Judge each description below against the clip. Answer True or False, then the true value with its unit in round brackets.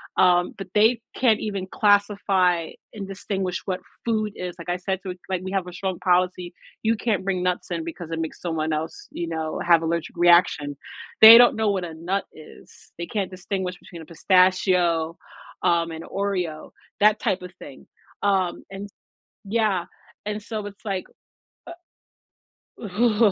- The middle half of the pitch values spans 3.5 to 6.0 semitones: False (2.9 semitones)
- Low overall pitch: False (185 Hz)